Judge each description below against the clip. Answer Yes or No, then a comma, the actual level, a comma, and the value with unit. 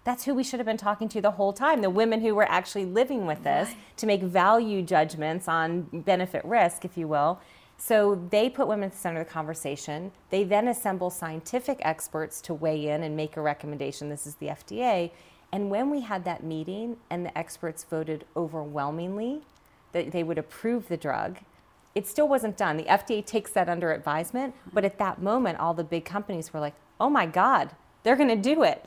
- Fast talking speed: Yes, fast, 210 wpm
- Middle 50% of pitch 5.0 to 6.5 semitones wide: Yes, wide, 5.6 semitones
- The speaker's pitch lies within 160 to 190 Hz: Yes, medium, 185 Hz